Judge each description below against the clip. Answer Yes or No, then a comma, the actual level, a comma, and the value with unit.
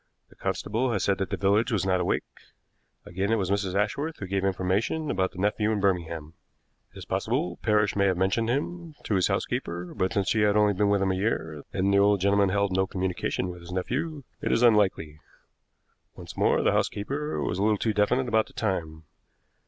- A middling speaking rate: No, fast, 210 wpm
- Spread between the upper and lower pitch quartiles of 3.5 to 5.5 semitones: No, narrow, 2.6 semitones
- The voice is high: No, low, 100 Hz